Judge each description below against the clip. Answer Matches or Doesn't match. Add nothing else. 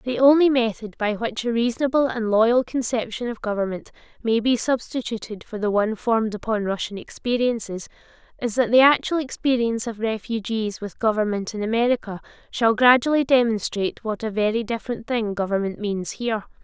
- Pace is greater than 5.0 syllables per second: Matches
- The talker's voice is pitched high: Matches